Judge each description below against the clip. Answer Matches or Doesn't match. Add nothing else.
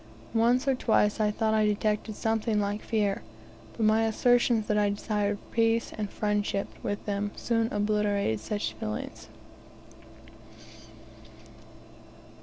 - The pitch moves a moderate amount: Doesn't match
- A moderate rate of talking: Doesn't match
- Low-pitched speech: Doesn't match